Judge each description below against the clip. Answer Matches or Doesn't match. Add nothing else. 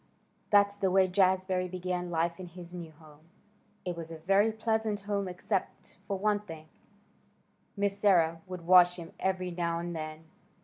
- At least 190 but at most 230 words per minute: Doesn't match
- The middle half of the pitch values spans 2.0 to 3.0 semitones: Matches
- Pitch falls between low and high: Matches